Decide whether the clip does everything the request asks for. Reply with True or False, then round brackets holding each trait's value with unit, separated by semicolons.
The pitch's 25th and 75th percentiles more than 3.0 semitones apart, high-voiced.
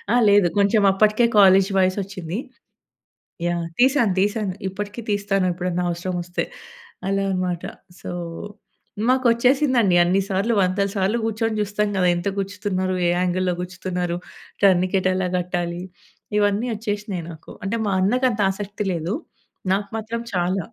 False (2.4 semitones; 195 Hz)